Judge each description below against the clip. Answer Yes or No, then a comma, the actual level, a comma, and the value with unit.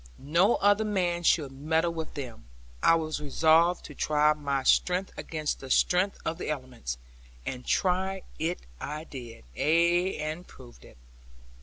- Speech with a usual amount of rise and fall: Yes, average, 3.8 semitones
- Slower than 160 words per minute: Yes, average, 150 wpm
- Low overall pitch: No, medium, 160 Hz